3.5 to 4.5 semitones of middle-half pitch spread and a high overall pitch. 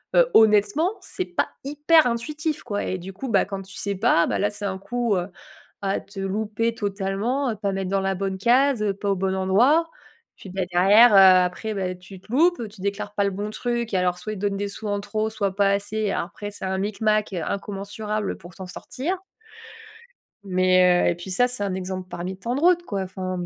No: average, 2.9 semitones; high, 200 Hz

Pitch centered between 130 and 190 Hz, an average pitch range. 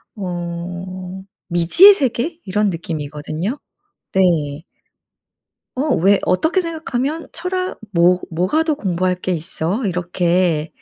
No: medium, 185 Hz; wide, 7.1 semitones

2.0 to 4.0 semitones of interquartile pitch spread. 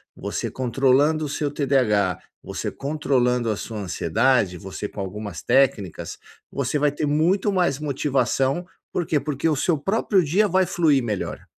No: average, 4.8 semitones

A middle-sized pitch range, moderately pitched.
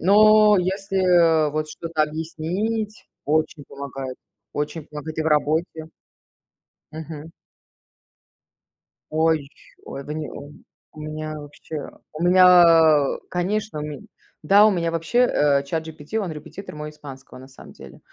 Yes: average, 3.0 semitones; medium, 160 Hz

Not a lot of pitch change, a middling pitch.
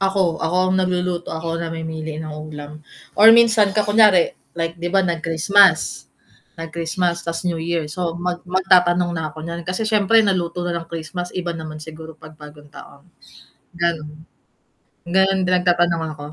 Yes: narrow, 2.3 semitones; medium, 170 Hz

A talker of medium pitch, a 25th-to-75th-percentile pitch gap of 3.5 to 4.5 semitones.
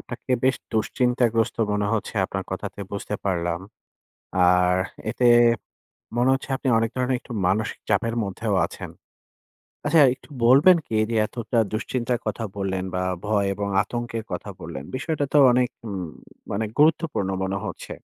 No: low, 110 Hz; average, 4.2 semitones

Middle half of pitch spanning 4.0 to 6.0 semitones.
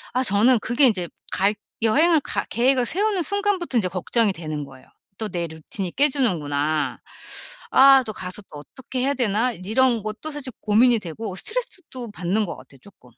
No: wide, 6.4 semitones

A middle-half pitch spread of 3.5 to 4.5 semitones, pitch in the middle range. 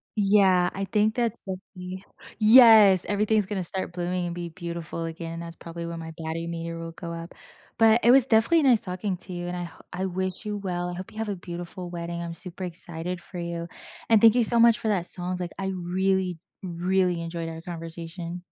No: average, 2.8 semitones; medium, 180 Hz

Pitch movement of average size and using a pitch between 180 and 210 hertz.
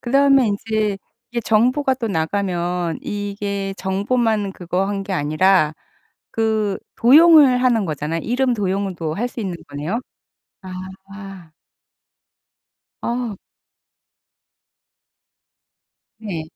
Yes: average, 4.1 semitones; high, 200 Hz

